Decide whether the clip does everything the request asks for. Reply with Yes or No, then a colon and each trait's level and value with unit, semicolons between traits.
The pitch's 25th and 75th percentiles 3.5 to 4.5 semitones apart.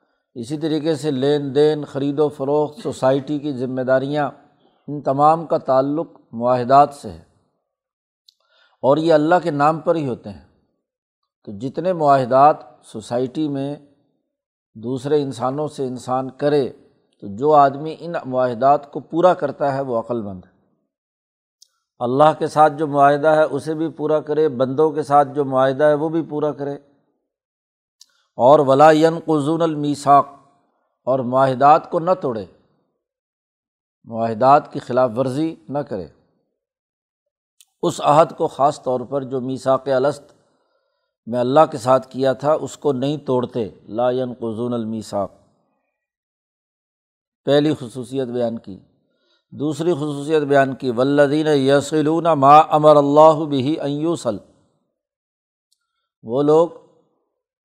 No: average, 3.0 semitones